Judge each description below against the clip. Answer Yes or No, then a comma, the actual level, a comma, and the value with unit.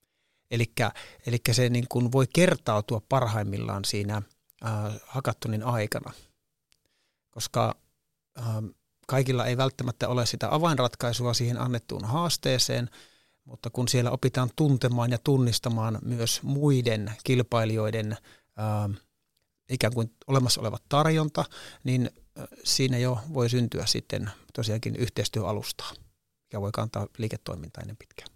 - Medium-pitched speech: No, low, 120 Hz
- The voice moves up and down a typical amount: Yes, average, 3.0 semitones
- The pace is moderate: Yes, average, 110 wpm